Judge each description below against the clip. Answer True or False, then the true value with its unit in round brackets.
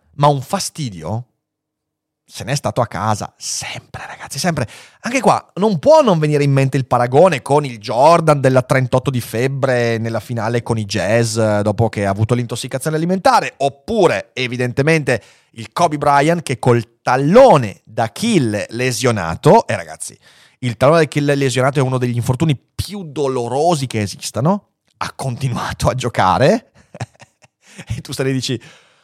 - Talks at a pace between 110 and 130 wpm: False (155 wpm)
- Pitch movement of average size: True (4.2 semitones)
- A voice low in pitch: True (130 Hz)